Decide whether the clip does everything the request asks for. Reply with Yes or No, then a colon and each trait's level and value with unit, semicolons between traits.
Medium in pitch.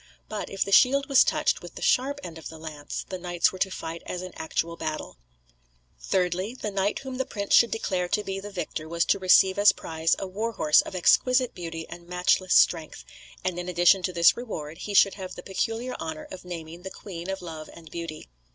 Yes: medium, 180 Hz